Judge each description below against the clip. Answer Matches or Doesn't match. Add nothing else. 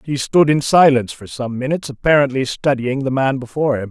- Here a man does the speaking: Matches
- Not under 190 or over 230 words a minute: Matches